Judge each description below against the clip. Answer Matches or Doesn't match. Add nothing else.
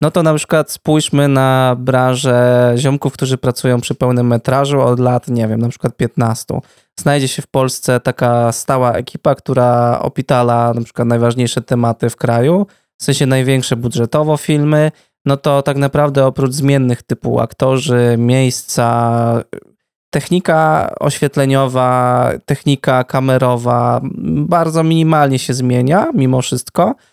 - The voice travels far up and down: Doesn't match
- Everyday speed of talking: Matches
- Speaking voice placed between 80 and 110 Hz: Doesn't match